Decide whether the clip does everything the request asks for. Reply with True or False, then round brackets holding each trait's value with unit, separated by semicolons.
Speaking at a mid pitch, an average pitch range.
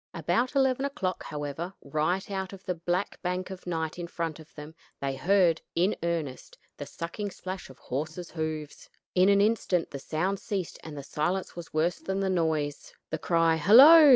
True (175 Hz; 3.5 semitones)